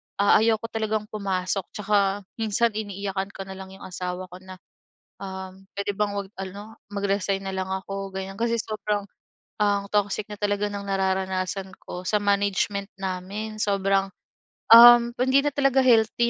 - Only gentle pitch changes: Yes, narrow, 1.7 semitones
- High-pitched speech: Yes, high, 200 Hz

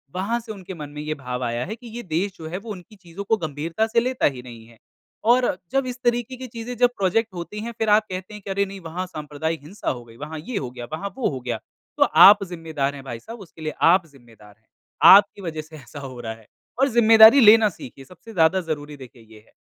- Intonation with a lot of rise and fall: Yes, wide, 7.2 semitones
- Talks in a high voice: No, medium, 175 Hz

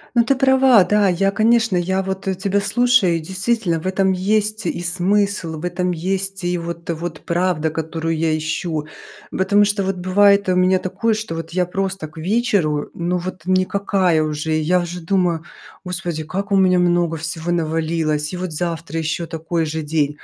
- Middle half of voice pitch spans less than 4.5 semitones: Yes, average, 3.1 semitones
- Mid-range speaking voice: Yes, medium, 180 Hz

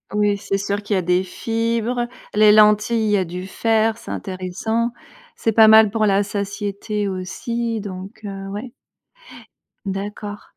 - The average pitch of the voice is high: Yes, high, 205 Hz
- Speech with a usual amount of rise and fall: No, narrow, 2.2 semitones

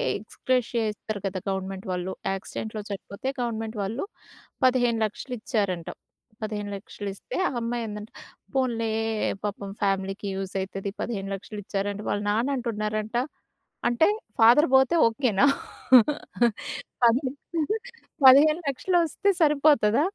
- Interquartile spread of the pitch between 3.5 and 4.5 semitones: Yes, average, 4.1 semitones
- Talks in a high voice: Yes, high, 220 Hz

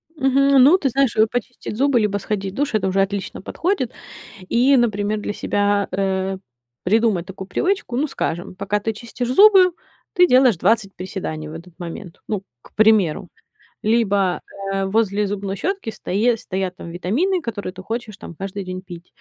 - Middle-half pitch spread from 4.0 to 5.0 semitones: Yes, average, 4.3 semitones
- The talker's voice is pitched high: Yes, high, 205 Hz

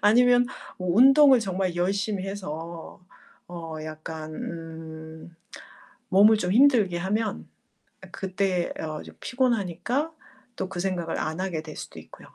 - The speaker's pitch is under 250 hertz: Yes, medium, 185 Hz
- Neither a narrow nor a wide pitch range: Yes, average, 4.7 semitones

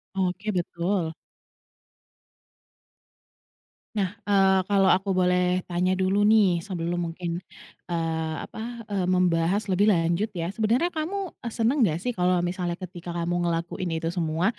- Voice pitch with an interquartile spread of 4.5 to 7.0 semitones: No, average, 2.8 semitones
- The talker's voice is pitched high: No, medium, 180 Hz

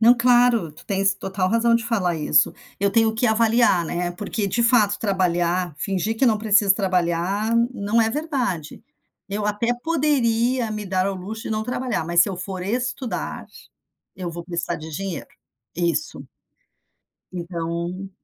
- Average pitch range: Yes, average, 4.5 semitones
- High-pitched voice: Yes, high, 200 Hz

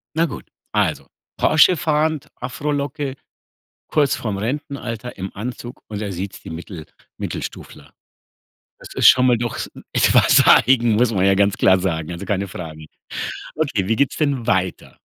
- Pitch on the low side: Yes, low, 115 Hz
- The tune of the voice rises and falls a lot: Yes, wide, 6.6 semitones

